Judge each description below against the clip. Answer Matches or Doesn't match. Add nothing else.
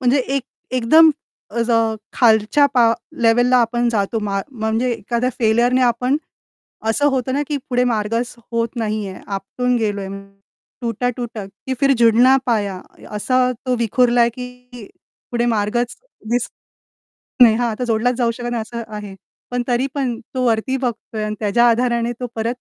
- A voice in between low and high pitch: Doesn't match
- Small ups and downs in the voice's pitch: Matches